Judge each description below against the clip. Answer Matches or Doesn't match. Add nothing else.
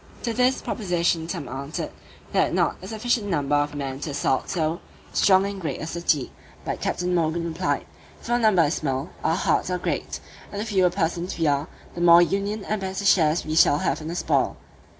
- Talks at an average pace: Doesn't match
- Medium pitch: Matches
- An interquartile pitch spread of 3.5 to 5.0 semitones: Matches